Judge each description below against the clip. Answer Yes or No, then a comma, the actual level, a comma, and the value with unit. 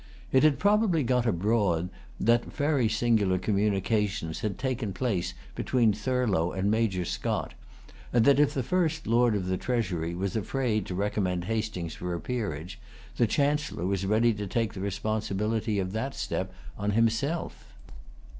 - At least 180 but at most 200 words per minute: No, average, 155 wpm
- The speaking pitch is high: No, low, 110 Hz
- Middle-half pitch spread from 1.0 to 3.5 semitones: No, average, 4.5 semitones